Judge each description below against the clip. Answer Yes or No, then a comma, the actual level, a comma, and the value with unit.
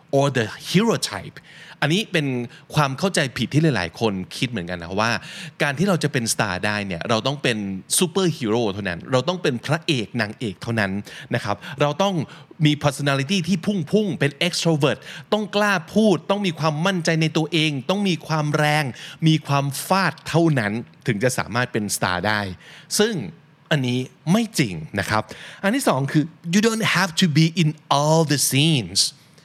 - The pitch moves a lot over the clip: Yes, wide, 6.3 semitones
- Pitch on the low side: No, medium, 150 Hz